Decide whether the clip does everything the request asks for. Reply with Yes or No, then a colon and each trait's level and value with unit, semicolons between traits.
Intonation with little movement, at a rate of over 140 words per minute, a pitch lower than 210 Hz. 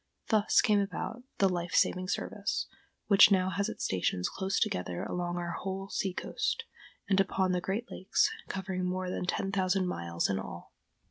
Yes: narrow, 1.7 semitones; average, 175 wpm; medium, 185 Hz